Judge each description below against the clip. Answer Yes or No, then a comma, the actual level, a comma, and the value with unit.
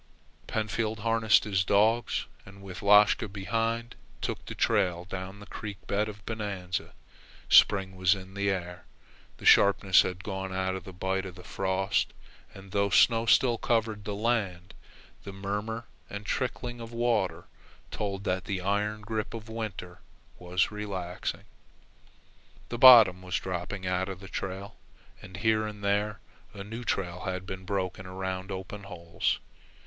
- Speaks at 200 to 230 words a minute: No, average, 155 wpm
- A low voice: Yes, low, 100 Hz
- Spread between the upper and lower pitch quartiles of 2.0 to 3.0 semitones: Yes, narrow, 2.4 semitones